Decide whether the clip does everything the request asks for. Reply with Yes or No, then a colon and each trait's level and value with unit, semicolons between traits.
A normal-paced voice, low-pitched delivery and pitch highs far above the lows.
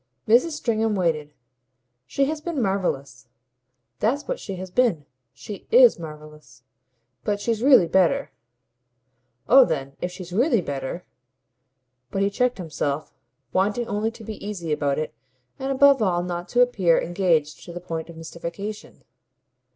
No: average, 150 wpm; medium, 185 Hz; wide, 6.7 semitones